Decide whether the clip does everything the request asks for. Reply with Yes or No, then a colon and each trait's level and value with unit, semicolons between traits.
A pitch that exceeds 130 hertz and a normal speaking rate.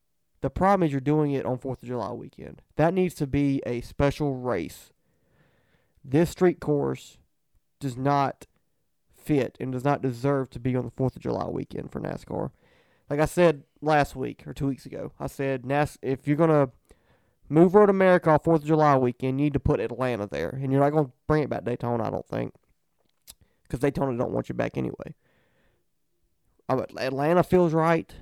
Yes: medium, 140 Hz; average, 195 wpm